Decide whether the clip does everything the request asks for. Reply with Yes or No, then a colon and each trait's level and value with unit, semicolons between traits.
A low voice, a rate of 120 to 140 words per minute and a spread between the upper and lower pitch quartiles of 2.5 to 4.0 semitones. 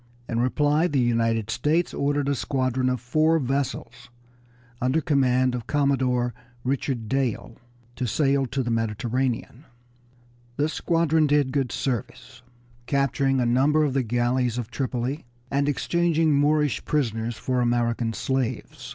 Yes: low, 130 Hz; slow, 135 wpm; average, 3.1 semitones